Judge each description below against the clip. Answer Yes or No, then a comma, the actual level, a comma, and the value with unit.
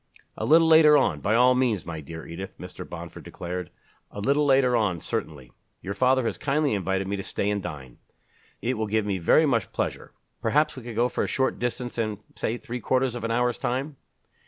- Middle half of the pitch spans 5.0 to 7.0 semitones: Yes, wide, 5.4 semitones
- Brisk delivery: Yes, fast, 210 wpm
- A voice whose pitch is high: No, low, 115 Hz